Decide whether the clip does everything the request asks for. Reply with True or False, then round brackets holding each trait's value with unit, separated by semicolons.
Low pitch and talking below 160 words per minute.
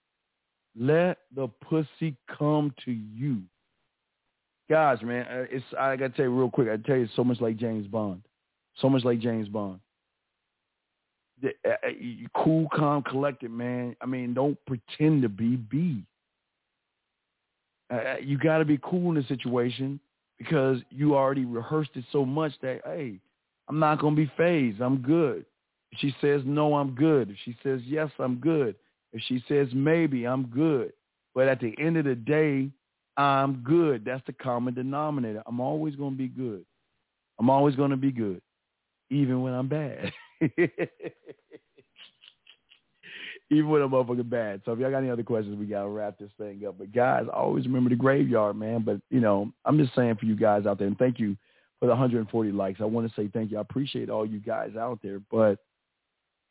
False (130 Hz; 175 wpm)